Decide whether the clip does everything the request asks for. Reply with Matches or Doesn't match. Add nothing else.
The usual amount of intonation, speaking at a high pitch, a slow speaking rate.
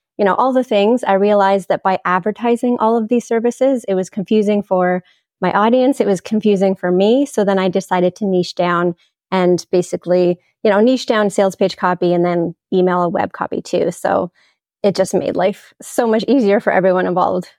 Doesn't match